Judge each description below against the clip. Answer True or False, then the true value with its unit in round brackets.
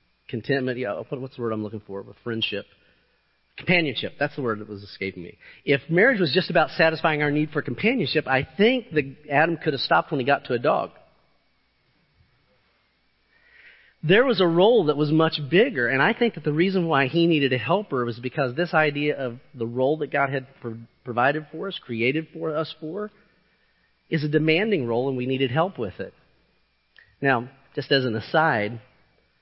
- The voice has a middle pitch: True (145 Hz)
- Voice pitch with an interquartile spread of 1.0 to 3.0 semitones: False (4.8 semitones)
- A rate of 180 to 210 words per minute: True (185 wpm)